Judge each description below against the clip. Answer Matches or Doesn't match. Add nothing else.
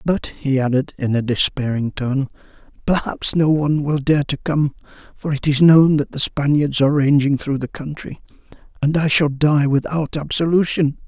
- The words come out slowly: Doesn't match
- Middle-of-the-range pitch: Matches